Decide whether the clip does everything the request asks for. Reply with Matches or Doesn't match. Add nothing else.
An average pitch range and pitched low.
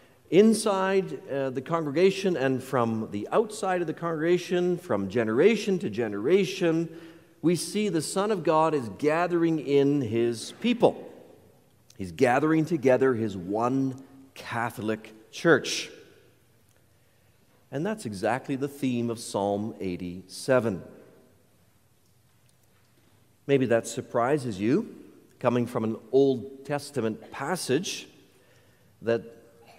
Doesn't match